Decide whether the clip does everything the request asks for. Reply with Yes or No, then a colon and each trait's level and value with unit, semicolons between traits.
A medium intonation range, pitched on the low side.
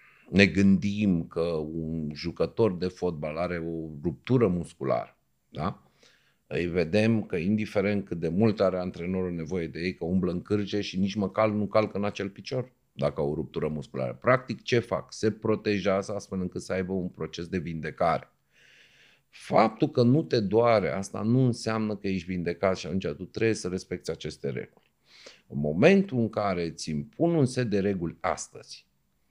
Yes: average, 4.1 semitones; very low, 95 Hz